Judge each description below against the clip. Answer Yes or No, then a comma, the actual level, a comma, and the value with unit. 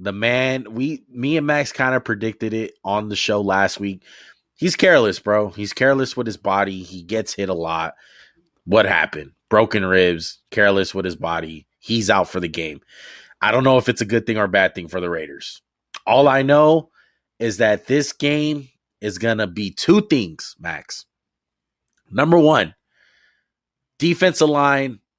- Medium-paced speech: Yes, average, 170 wpm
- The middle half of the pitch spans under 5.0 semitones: No, wide, 5.4 semitones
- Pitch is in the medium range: No, low, 110 Hz